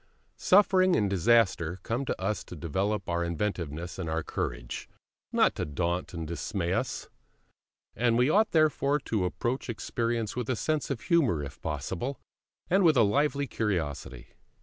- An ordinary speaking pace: Yes, average, 155 wpm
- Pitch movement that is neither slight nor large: No, wide, 7.7 semitones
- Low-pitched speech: Yes, low, 105 Hz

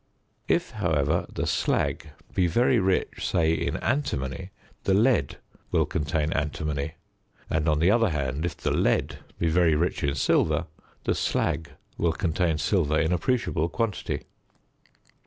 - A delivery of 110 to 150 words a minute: Yes, average, 140 wpm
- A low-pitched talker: Yes, very low, 80 Hz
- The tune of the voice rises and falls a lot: No, average, 3.6 semitones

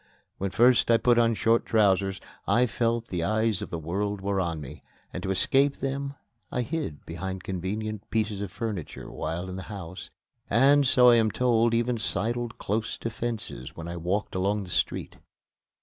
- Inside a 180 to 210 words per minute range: Yes, average, 185 wpm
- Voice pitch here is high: No, low, 110 Hz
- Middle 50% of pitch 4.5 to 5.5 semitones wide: No, average, 3.9 semitones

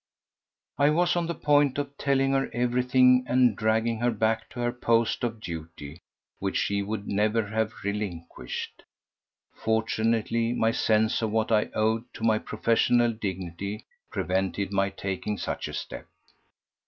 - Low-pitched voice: Yes, low, 110 Hz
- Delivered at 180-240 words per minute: No, average, 150 wpm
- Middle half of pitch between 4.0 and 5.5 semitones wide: No, average, 3.2 semitones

